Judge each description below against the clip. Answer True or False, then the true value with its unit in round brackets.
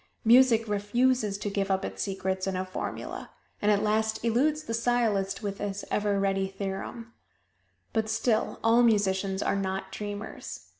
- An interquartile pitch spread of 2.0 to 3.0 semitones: True (2.7 semitones)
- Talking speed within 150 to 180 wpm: True (155 wpm)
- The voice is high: True (205 Hz)